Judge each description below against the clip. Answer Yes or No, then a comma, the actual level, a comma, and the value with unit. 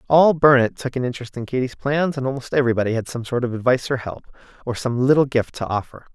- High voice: No, low, 125 Hz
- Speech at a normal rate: No, fast, 235 wpm